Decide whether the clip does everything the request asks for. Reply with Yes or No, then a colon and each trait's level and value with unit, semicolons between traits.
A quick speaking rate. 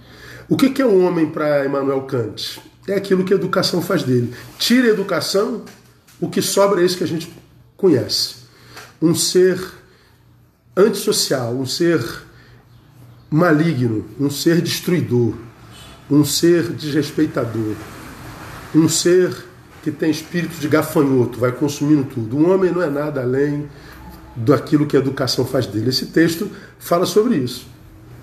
No: average, 145 wpm